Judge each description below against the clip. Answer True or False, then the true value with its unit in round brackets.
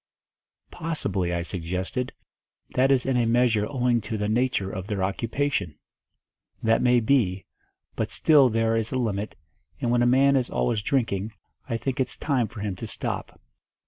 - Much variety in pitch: False (4.2 semitones)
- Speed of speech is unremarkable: True (170 wpm)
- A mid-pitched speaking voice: False (115 Hz)